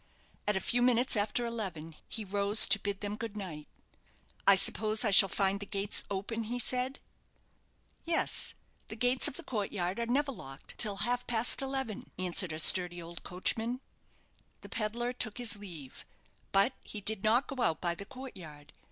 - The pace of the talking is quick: No, average, 180 wpm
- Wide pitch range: No, average, 3.9 semitones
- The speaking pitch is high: Yes, high, 210 Hz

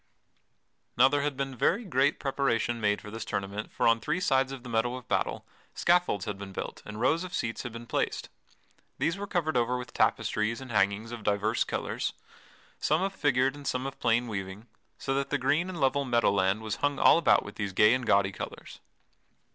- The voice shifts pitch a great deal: No, average, 4.6 semitones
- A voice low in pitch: Yes, low, 125 Hz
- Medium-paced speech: No, fast, 210 wpm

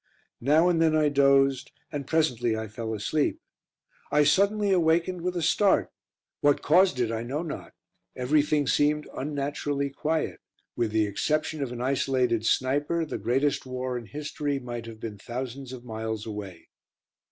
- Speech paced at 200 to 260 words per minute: No, average, 155 wpm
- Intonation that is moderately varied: Yes, average, 4.2 semitones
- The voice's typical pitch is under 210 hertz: Yes, medium, 140 Hz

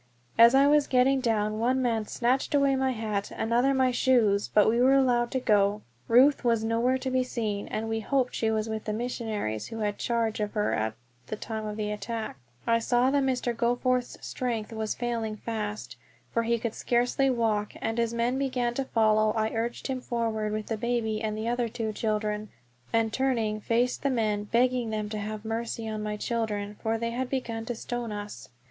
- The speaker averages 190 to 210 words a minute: Yes, average, 200 wpm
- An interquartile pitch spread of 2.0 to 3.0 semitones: Yes, narrow, 2.4 semitones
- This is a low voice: No, high, 230 Hz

